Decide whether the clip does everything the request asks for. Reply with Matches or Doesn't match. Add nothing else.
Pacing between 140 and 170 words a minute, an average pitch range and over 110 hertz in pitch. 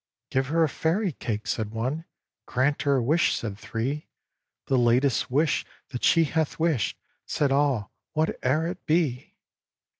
Matches